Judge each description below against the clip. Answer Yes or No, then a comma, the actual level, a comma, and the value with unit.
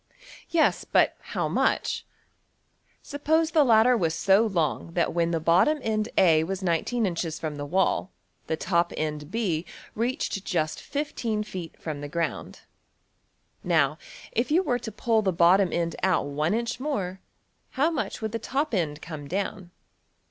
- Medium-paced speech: Yes, average, 145 wpm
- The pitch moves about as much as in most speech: No, wide, 5.9 semitones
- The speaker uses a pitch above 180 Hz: Yes, high, 190 Hz